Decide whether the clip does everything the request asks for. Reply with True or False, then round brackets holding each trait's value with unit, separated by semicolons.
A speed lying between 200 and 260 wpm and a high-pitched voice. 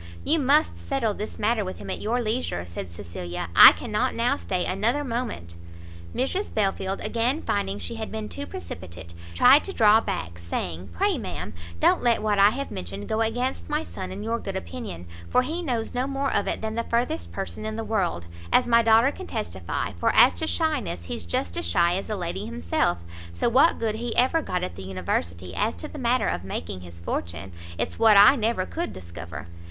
True (205 wpm; 210 Hz)